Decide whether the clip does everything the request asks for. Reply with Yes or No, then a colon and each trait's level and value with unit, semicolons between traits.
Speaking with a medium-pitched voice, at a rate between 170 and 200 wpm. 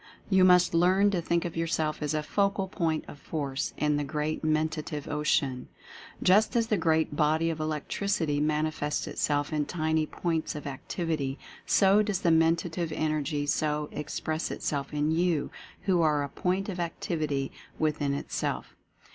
No: medium, 155 Hz; average, 155 wpm